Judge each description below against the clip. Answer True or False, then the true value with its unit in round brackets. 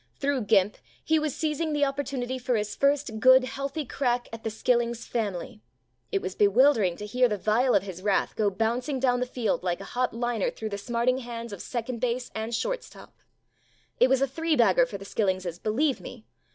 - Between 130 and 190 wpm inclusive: False (205 wpm)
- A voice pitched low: False (240 Hz)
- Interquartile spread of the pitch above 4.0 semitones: False (3.7 semitones)